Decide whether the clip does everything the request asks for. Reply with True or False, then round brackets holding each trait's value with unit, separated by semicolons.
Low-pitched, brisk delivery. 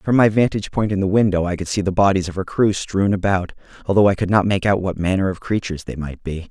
True (95 Hz; 275 wpm)